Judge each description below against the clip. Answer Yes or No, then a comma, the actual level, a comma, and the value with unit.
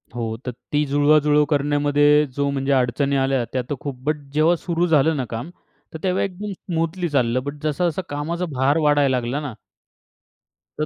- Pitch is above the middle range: No, medium, 145 Hz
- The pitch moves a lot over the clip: No, average, 2.7 semitones